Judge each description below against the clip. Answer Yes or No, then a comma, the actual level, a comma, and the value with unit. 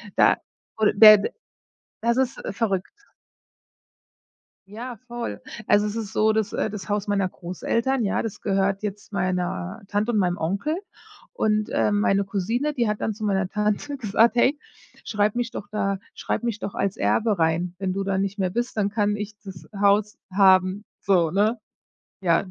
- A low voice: No, high, 205 Hz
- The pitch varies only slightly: Yes, narrow, 2.2 semitones